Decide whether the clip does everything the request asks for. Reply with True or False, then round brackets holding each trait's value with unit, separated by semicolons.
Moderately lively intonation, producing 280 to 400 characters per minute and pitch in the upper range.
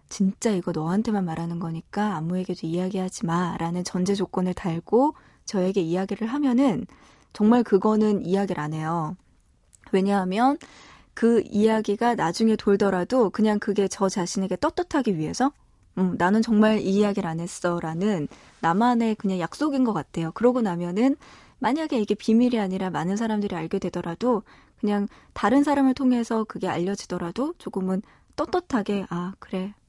True (3.8 semitones; 345 characters per minute; 200 Hz)